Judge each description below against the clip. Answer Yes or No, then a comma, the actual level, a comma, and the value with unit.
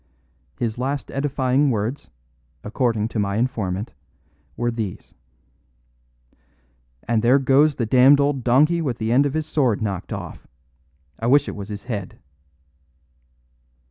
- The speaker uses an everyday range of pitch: Yes, average, 4.1 semitones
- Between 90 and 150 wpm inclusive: Yes, slow, 135 wpm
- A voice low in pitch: Yes, low, 125 Hz